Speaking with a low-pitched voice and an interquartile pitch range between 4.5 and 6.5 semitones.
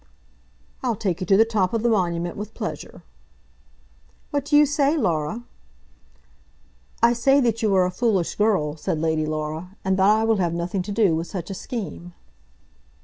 No: high, 195 Hz; average, 4.9 semitones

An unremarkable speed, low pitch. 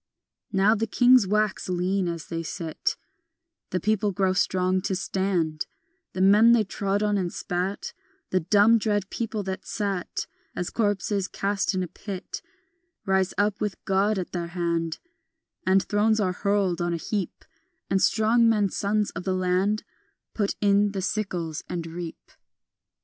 No: average, 155 wpm; high, 195 Hz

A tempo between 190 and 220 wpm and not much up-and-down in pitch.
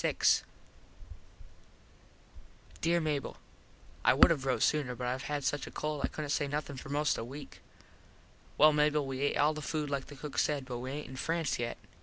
Yes: average, 195 wpm; narrow, 2.1 semitones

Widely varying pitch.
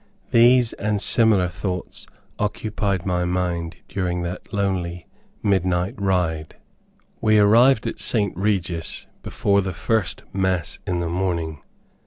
No: average, 2.8 semitones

